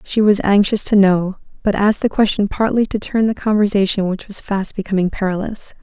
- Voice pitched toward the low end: No, high, 200 Hz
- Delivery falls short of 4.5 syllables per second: No, 5.5 syllables/s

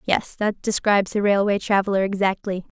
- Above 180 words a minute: No, average, 150 wpm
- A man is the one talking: No, female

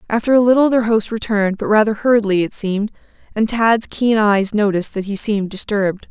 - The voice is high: Yes, high, 210 Hz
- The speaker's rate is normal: Yes, average, 195 wpm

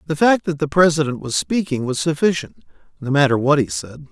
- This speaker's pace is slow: No, fast, 205 wpm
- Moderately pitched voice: Yes, medium, 150 Hz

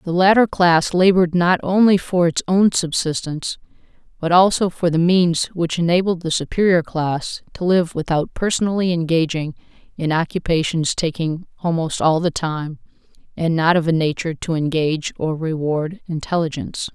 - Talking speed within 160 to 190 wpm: No, average, 150 wpm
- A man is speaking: No, female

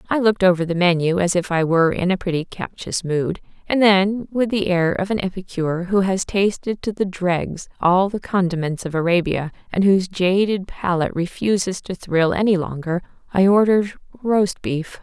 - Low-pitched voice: No, medium, 185 Hz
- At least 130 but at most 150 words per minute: No, average, 185 wpm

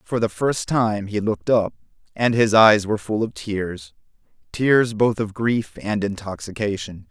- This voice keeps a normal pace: Yes, average, 160 wpm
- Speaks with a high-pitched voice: No, low, 105 Hz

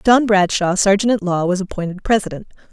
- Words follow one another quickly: No, average, 175 wpm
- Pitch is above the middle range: Yes, high, 195 Hz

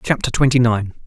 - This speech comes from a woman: No, male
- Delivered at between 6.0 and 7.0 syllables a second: No, 5.8 syllables/s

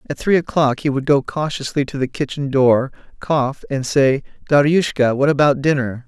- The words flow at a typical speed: Yes, average, 180 wpm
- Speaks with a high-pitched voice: No, medium, 140 Hz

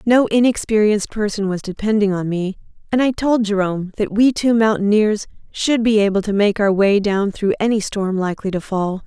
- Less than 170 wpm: No, average, 190 wpm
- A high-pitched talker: Yes, high, 205 Hz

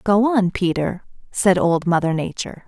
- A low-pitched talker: No, medium, 185 Hz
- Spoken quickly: No, average, 155 wpm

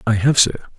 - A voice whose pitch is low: Yes, low, 115 Hz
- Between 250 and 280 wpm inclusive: No, fast, 230 wpm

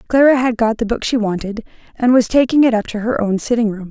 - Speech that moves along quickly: Yes, fast, 260 wpm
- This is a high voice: Yes, high, 230 Hz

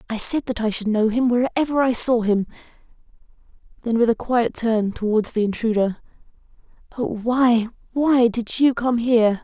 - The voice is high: Yes, high, 235 Hz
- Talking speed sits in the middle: Yes, average, 165 wpm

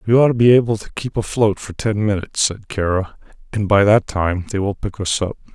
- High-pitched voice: No, low, 105 Hz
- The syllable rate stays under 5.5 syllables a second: No, 5.6 syllables/s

